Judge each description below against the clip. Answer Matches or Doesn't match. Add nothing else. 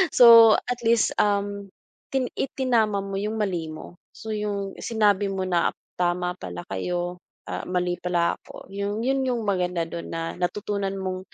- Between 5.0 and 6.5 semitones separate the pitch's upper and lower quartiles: Doesn't match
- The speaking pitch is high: Matches